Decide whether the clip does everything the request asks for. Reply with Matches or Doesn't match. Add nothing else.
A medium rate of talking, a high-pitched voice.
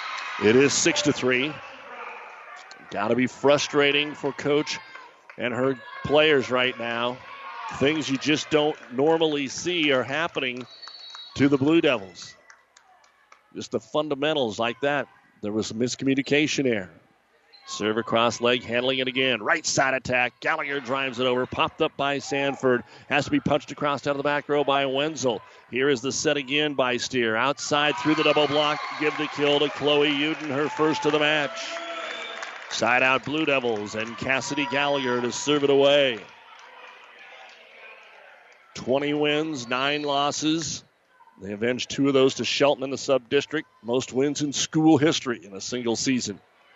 Doesn't match